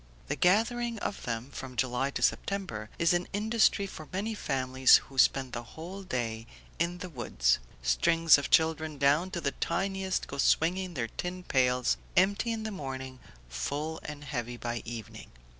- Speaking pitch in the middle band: Yes, medium, 150 Hz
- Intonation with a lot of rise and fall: Yes, wide, 6.6 semitones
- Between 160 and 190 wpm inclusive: Yes, average, 165 wpm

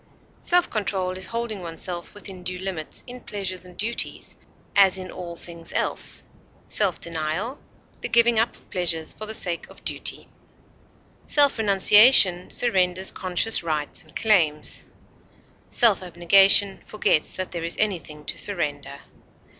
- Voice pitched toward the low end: No, medium, 185 Hz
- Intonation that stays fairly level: No, average, 3.7 semitones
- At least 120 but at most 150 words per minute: Yes, average, 140 wpm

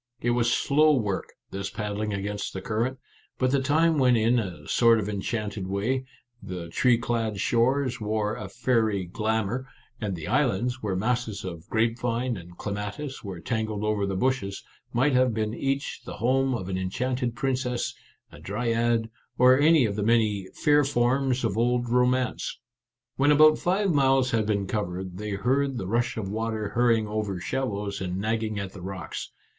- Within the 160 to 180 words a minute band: Yes, average, 175 wpm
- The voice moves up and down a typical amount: Yes, average, 3.9 semitones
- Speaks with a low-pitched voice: Yes, low, 115 Hz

